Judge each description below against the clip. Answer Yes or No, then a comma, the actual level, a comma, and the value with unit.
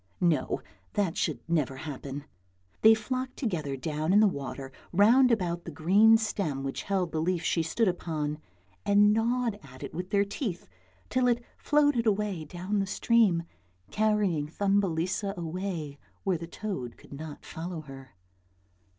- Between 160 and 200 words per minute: No, average, 150 wpm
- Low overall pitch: No, medium, 180 Hz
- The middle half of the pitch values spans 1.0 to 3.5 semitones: No, average, 5.1 semitones